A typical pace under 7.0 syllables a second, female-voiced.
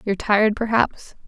Yes: 5.7 syllables/s; female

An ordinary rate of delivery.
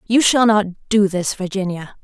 Yes: average, 175 wpm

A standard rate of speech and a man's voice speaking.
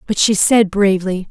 No: average, 185 wpm; female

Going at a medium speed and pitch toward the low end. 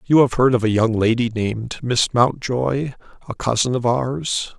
Yes: average, 185 wpm; low, 120 Hz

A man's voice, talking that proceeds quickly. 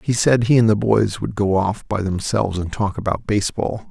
Yes: male; fast, 230 wpm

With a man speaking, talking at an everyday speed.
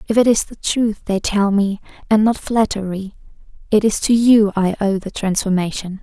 No: female; average, 190 wpm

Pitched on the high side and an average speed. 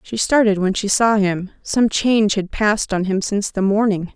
No: high, 205 Hz; fast, 215 wpm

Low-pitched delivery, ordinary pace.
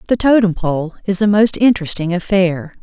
No: high, 190 Hz; average, 170 wpm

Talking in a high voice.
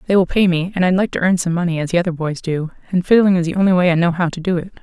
No: medium, 175 Hz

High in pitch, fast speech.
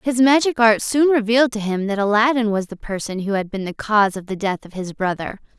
Yes: high, 215 Hz; fast, 245 wpm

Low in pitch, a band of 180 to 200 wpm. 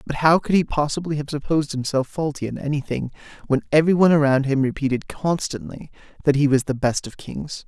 No: medium, 145 Hz; average, 190 wpm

